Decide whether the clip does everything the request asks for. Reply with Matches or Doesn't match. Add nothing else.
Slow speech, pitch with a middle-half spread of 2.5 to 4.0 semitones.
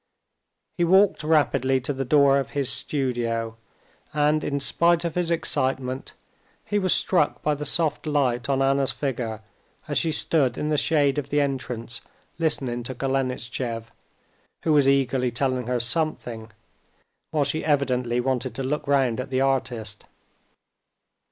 Doesn't match